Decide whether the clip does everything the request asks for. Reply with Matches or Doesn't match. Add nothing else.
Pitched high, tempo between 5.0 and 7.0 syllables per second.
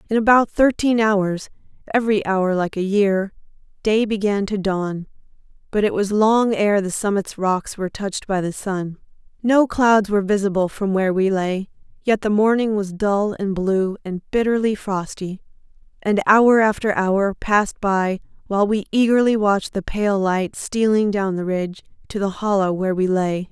Doesn't match